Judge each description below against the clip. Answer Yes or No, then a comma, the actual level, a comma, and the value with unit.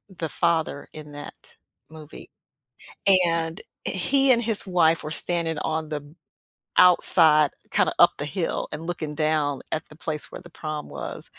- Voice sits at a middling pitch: Yes, medium, 160 Hz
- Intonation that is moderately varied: No, narrow, 2.2 semitones